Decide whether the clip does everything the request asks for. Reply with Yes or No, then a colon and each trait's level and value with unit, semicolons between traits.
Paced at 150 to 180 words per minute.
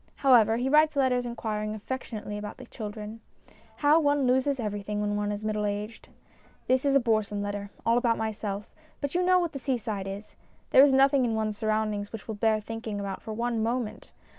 No: average, 195 wpm